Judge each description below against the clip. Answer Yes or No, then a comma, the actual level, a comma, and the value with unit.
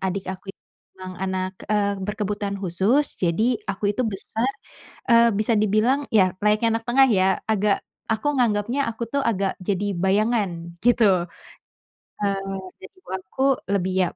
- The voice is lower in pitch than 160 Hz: No, high, 205 Hz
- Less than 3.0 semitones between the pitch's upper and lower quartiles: No, average, 3.3 semitones